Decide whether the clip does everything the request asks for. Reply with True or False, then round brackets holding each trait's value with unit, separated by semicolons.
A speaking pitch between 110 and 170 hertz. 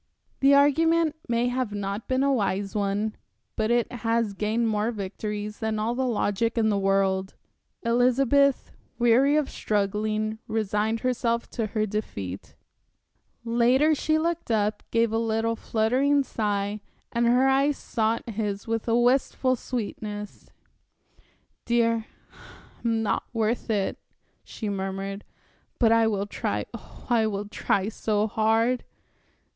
False (225 Hz)